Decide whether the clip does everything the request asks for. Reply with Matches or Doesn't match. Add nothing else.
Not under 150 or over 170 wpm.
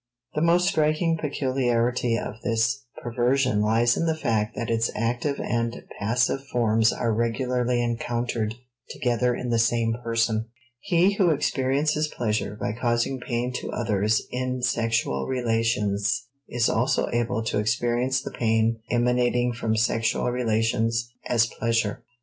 Doesn't match